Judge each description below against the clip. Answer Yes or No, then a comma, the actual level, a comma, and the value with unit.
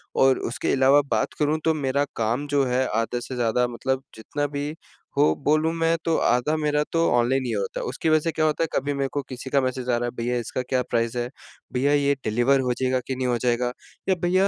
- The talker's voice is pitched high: No, low, 130 Hz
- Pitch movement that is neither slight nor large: Yes, average, 3.1 semitones